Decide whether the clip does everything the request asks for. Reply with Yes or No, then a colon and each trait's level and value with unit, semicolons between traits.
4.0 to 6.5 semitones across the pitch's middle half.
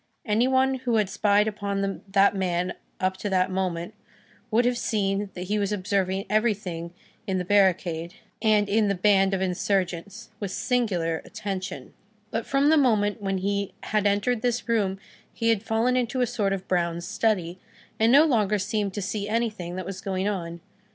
No: average, 2.8 semitones